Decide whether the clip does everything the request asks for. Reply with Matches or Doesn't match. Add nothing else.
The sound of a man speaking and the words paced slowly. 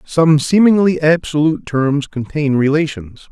Matches